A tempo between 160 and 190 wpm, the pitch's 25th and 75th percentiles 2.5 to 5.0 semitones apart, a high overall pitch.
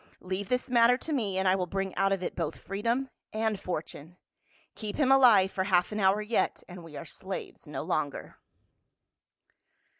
Yes: average, 180 wpm; average, 3.8 semitones; high, 195 Hz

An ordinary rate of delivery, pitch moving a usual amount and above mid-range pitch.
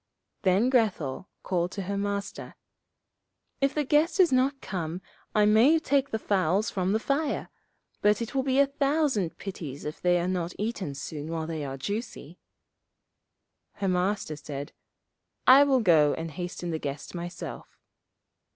No: average, 155 wpm; wide, 7.4 semitones; high, 195 Hz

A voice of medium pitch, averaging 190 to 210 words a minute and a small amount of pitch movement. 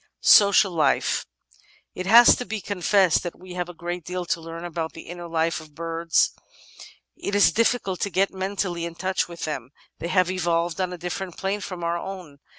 Yes: medium, 175 Hz; average, 195 wpm; narrow, 2.3 semitones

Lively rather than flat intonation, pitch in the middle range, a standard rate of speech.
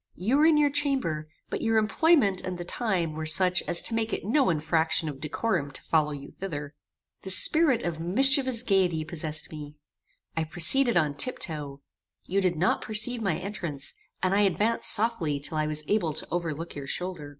Yes: wide, 6.3 semitones; medium, 180 Hz; average, 185 wpm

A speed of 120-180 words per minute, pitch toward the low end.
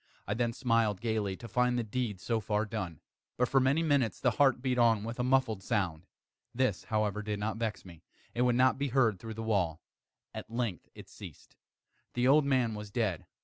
No: fast, 205 wpm; low, 115 Hz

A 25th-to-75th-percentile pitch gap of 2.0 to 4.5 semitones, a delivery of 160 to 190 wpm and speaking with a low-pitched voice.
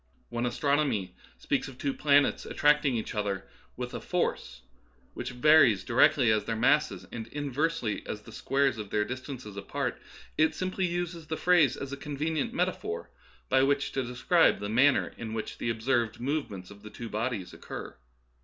No: average, 5.1 semitones; average, 180 wpm; low, 130 Hz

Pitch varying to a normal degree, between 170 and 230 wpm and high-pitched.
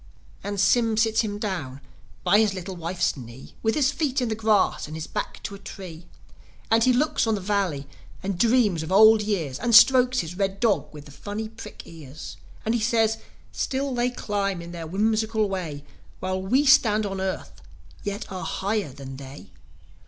Yes: average, 4.3 semitones; average, 190 wpm; high, 205 Hz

